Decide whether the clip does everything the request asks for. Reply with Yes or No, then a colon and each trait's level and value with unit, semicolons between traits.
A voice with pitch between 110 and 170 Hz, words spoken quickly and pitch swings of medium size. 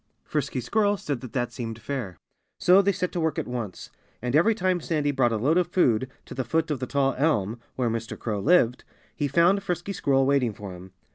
No: low, 135 Hz; fast, 220 wpm; wide, 6.3 semitones